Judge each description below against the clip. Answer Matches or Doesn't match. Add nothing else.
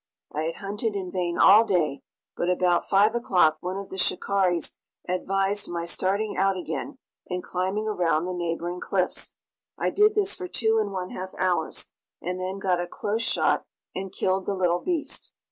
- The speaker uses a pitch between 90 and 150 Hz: Doesn't match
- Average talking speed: Matches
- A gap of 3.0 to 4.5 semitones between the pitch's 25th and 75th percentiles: Doesn't match